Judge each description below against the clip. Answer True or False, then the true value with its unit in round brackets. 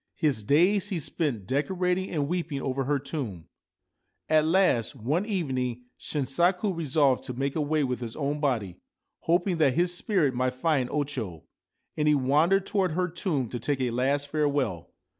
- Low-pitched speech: False (145 Hz)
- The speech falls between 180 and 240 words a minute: False (165 wpm)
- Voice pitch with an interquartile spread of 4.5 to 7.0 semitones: True (4.9 semitones)